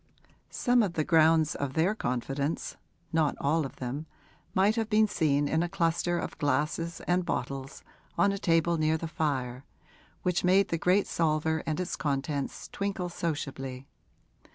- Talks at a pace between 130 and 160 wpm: Yes, average, 155 wpm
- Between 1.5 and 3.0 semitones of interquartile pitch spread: No, average, 3.8 semitones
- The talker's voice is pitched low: No, medium, 160 Hz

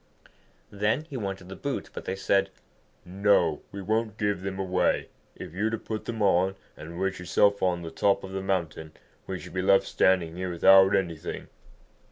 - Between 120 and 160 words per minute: No, average, 190 wpm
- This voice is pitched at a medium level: No, very low, 95 Hz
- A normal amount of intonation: No, narrow, 2.1 semitones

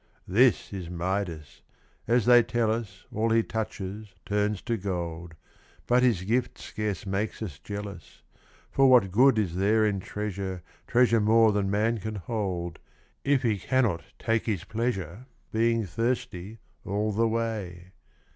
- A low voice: Yes, low, 105 Hz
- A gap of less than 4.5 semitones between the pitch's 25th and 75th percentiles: Yes, average, 3.4 semitones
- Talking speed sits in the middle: Yes, average, 145 wpm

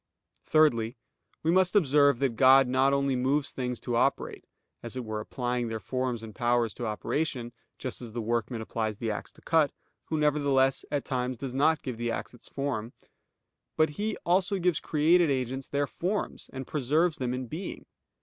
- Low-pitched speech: Yes, low, 130 Hz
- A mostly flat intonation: No, average, 3.8 semitones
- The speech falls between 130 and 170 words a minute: No, average, 180 wpm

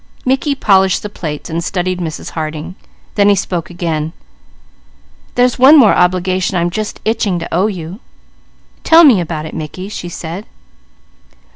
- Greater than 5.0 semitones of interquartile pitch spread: No, average, 3.9 semitones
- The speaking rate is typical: Yes, average, 150 wpm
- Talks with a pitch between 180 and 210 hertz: Yes, medium, 185 Hz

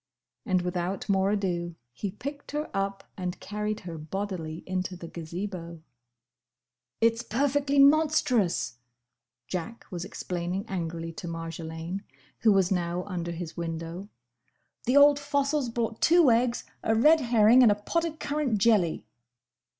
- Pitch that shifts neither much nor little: No, wide, 5.8 semitones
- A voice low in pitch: No, high, 195 Hz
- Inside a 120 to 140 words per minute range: Yes, slow, 135 wpm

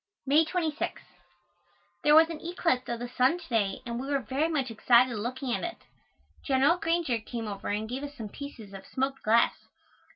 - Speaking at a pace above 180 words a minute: Yes, average, 190 wpm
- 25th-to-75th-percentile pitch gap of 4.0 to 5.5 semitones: Yes, average, 4.6 semitones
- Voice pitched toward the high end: Yes, very high, 260 Hz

